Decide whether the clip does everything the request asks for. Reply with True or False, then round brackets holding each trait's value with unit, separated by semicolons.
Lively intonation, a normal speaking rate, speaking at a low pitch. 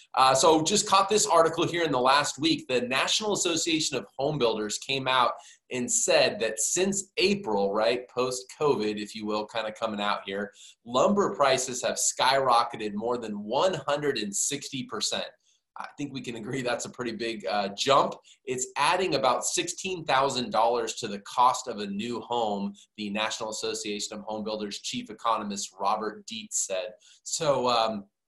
True (7.1 semitones; 165 wpm; 125 Hz)